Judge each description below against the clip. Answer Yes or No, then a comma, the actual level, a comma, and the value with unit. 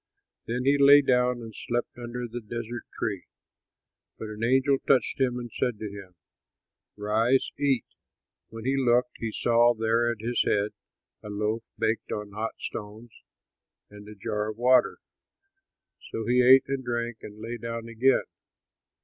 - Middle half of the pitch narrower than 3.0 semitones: Yes, narrow, 2.4 semitones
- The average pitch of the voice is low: Yes, low, 115 Hz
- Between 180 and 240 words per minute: No, average, 160 wpm